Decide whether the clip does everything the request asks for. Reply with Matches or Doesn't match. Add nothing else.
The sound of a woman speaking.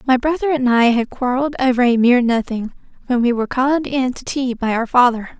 Matches